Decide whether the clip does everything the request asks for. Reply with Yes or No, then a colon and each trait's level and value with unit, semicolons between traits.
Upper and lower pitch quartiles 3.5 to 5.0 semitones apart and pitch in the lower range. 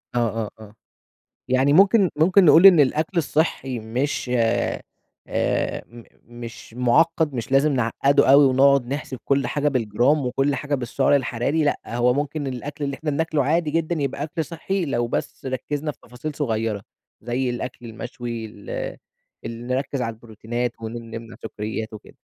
Yes: average, 3.8 semitones; low, 130 Hz